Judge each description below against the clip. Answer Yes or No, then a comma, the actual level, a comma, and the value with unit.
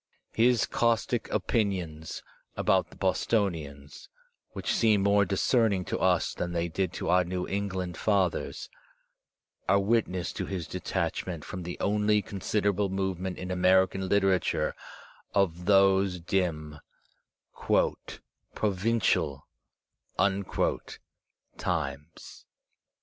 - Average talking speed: No, slow, 100 wpm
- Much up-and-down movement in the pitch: No, narrow, 2.4 semitones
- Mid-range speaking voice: No, very low, 95 Hz